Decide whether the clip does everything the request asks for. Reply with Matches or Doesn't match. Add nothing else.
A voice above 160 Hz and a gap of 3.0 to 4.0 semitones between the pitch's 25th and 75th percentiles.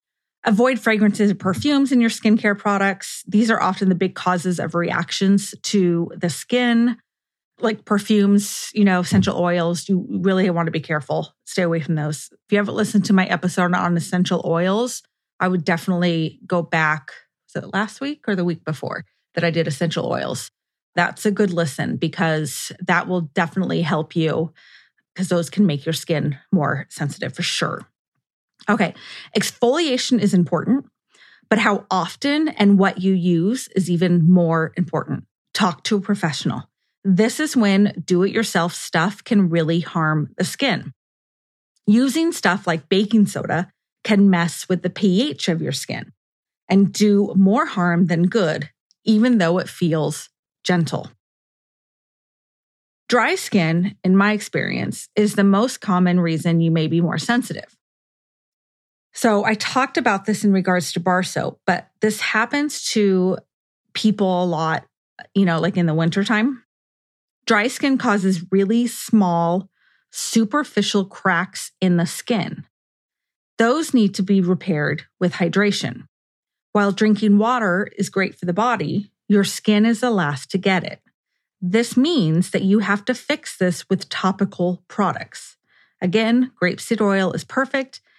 Matches